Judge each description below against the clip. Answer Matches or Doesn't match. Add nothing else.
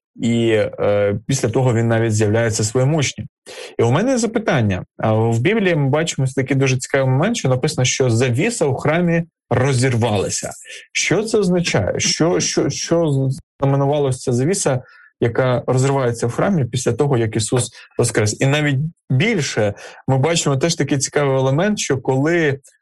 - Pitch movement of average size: Matches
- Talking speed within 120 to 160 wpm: Matches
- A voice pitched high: Doesn't match